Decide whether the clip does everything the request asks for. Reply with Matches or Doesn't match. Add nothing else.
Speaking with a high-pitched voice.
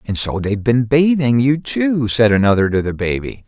Doesn't match